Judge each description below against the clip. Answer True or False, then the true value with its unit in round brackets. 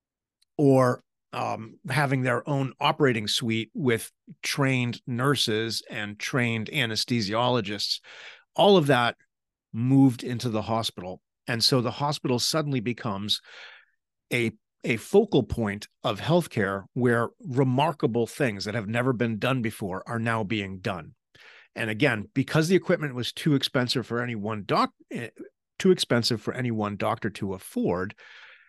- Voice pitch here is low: True (120 Hz)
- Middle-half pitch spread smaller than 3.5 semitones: False (4.1 semitones)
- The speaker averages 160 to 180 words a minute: False (135 wpm)